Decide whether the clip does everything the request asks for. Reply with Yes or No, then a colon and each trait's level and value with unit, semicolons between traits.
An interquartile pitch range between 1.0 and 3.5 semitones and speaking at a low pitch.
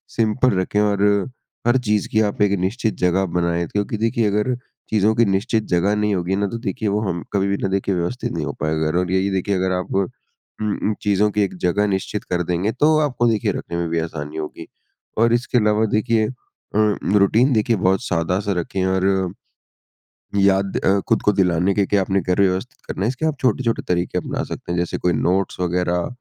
Yes: average, 3.0 semitones; low, 100 Hz